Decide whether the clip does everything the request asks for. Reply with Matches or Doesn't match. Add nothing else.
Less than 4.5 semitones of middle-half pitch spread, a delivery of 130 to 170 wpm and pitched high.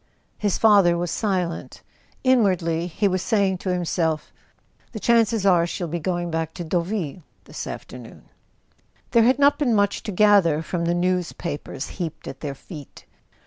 Doesn't match